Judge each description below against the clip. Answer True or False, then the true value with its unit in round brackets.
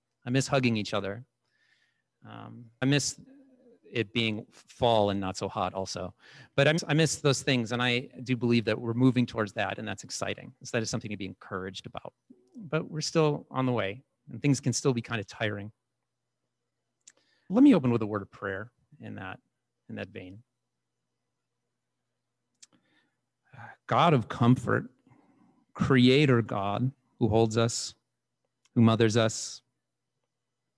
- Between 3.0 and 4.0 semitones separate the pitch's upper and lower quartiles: True (3.7 semitones)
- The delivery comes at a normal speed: True (160 wpm)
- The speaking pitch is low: True (120 Hz)